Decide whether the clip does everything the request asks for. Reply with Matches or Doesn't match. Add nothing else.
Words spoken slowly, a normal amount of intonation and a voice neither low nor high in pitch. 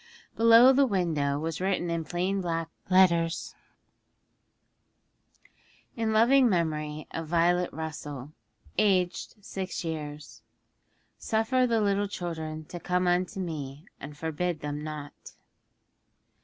Matches